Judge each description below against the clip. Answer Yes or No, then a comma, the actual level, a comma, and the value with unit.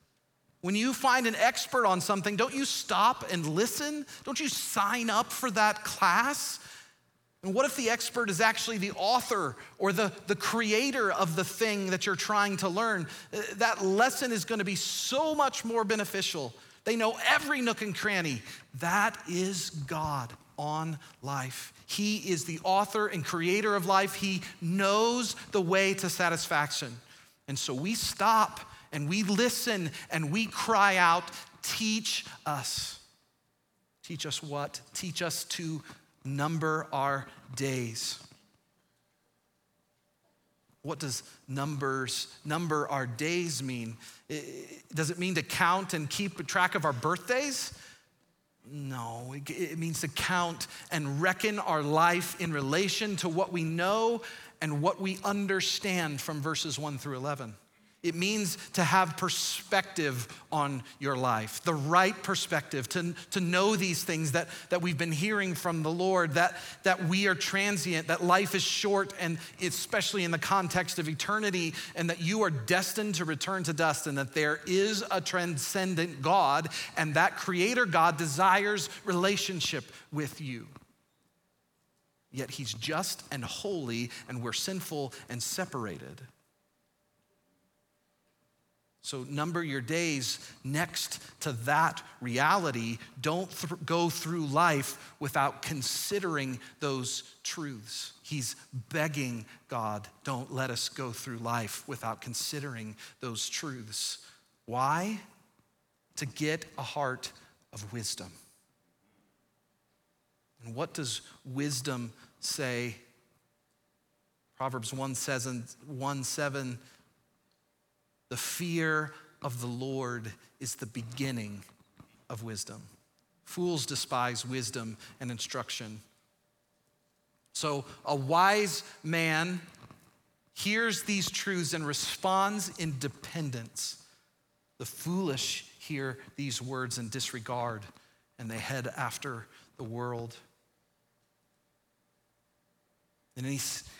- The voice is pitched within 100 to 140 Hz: No, medium, 165 Hz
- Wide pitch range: Yes, wide, 6.2 semitones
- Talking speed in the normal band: No, slow, 130 wpm